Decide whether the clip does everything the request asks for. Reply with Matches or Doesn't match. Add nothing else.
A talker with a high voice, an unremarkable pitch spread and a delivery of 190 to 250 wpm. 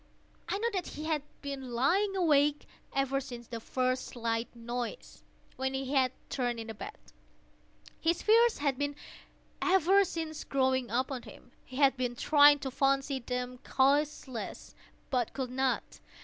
Doesn't match